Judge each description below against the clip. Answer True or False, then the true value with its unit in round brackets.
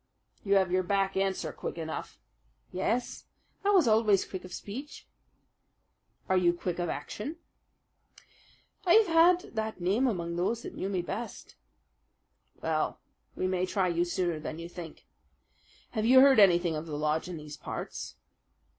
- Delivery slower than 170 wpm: True (155 wpm)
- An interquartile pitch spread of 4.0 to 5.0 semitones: True (4.3 semitones)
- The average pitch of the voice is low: False (185 Hz)